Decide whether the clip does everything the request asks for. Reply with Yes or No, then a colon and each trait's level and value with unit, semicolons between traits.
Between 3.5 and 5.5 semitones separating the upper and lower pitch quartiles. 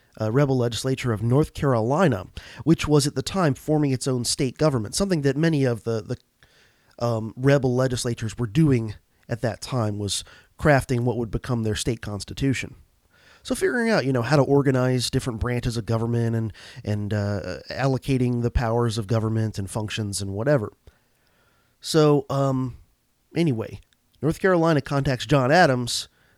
Yes: average, 4.0 semitones